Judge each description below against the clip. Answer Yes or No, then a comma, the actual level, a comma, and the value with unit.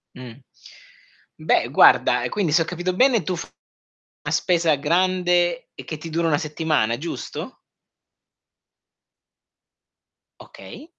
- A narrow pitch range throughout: No, average, 3.1 semitones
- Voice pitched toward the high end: No, medium, 165 Hz